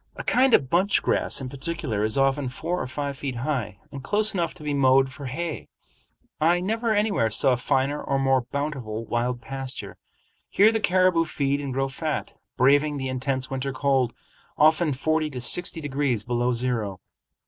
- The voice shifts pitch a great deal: No, average, 3.7 semitones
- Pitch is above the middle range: No, medium, 140 Hz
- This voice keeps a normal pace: Yes, average, 175 wpm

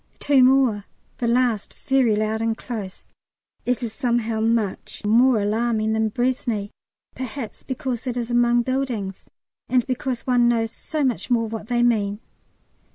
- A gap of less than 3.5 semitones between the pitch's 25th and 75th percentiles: Yes, narrow, 2.4 semitones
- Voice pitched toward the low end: No, high, 235 Hz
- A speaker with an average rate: Yes, average, 150 wpm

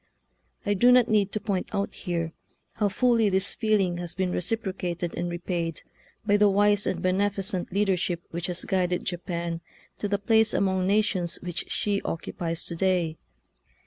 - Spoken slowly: No, average, 165 wpm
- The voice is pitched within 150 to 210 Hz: Yes, high, 190 Hz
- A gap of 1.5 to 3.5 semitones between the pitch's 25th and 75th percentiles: Yes, average, 2.8 semitones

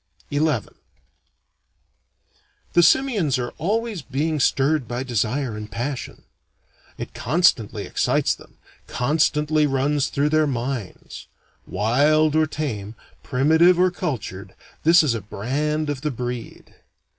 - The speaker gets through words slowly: Yes, slow, 115 wpm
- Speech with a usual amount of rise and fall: Yes, average, 4.1 semitones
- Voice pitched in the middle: Yes, medium, 145 Hz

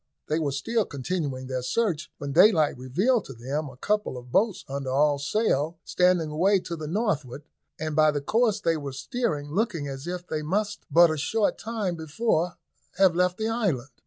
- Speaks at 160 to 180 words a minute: No, average, 190 wpm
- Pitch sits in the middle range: Yes, medium, 160 Hz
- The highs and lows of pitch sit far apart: Yes, wide, 6.2 semitones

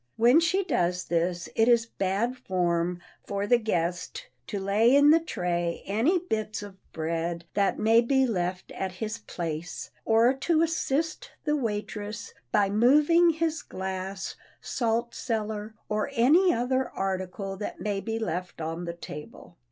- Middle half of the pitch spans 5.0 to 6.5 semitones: Yes, wide, 5.5 semitones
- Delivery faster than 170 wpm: No, average, 150 wpm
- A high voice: Yes, high, 215 Hz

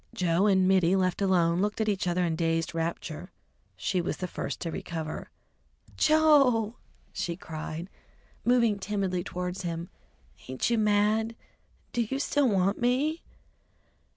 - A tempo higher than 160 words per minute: No, average, 140 wpm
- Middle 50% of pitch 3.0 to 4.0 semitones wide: No, average, 4.4 semitones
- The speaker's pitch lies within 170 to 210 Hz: Yes, high, 190 Hz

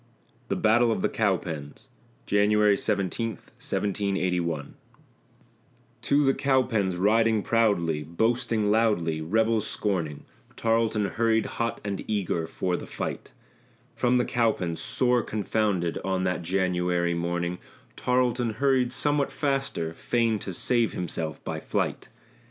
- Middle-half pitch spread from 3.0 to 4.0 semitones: No, average, 4.6 semitones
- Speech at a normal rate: No, slow, 115 wpm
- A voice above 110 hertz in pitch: No, low, 105 Hz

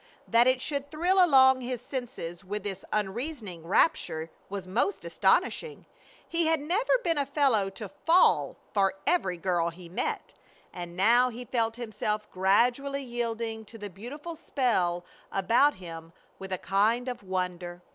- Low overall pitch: No, high, 225 Hz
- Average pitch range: No, wide, 6.4 semitones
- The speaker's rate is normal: Yes, average, 155 wpm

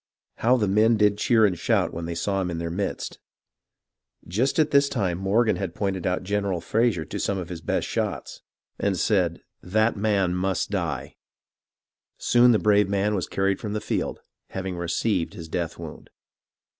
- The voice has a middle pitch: No, very low, 95 Hz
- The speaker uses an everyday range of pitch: Yes, average, 3.2 semitones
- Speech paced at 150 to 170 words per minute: No, average, 185 wpm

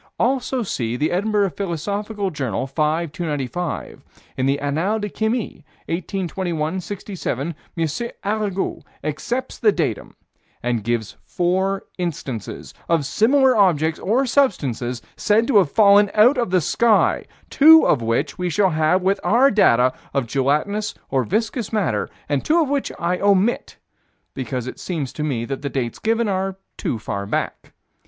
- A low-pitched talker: No, medium, 180 Hz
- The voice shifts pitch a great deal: Yes, wide, 7.0 semitones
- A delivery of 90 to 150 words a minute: Yes, average, 145 wpm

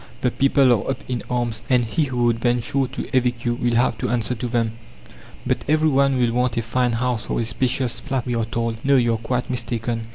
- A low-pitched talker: Yes, low, 120 Hz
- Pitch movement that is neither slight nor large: No, narrow, 1.8 semitones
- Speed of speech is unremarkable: No, fast, 235 wpm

